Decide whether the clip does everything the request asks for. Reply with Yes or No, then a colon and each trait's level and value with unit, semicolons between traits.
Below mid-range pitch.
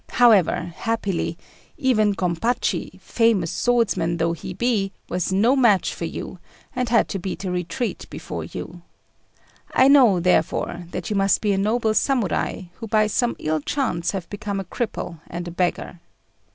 No: high, 200 Hz